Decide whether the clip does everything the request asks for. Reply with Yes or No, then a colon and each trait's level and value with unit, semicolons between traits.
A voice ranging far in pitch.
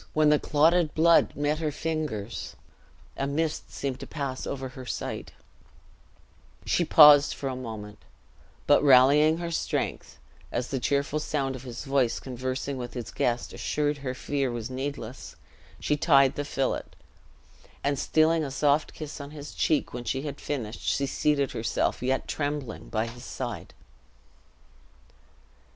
No: average, 2.7 semitones